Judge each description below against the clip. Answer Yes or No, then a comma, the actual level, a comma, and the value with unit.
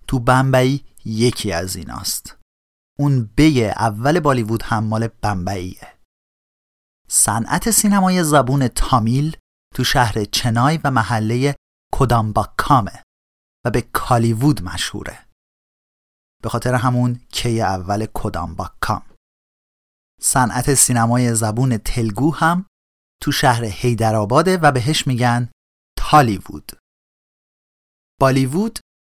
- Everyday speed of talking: No, slow, 95 wpm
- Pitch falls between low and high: No, low, 120 Hz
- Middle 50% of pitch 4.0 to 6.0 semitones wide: Yes, average, 4.9 semitones